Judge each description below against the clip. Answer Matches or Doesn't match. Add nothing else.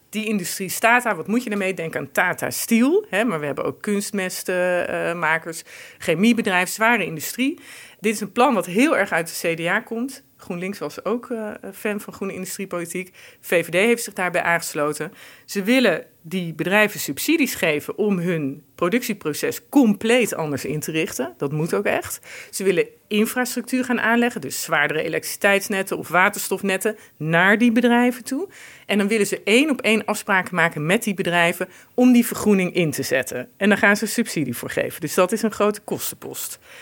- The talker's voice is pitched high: Matches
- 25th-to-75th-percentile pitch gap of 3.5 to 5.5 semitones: Matches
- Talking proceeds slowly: Doesn't match